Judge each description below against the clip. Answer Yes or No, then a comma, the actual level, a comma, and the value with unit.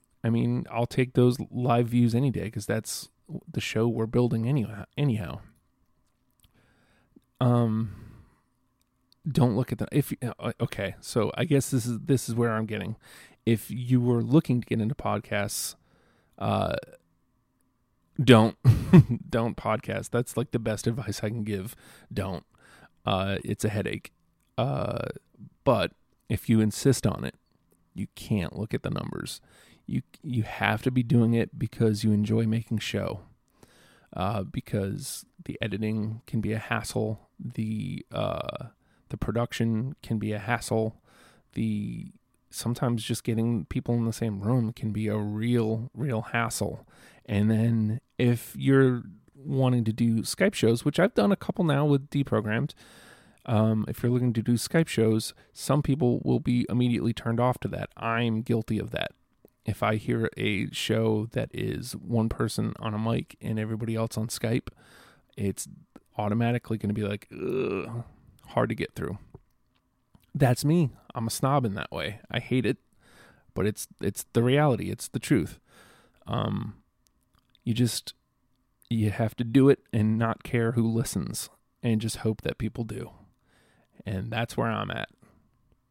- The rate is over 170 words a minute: No, average, 155 wpm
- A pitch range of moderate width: No, narrow, 2.2 semitones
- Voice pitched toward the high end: No, low, 115 Hz